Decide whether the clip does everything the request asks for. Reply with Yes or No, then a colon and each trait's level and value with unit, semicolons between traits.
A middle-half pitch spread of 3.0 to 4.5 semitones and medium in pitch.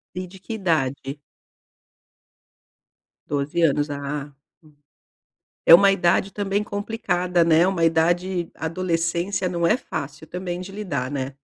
Yes: average, 4.0 semitones; medium, 170 Hz